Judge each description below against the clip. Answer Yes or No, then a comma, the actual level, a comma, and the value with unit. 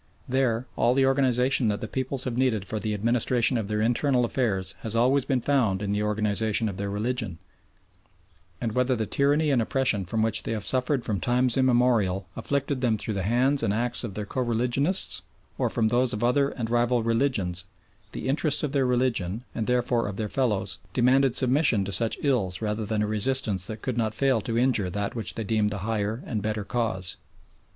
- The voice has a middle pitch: No, low, 115 Hz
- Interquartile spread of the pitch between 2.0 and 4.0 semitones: Yes, average, 3.4 semitones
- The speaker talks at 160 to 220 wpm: Yes, average, 200 wpm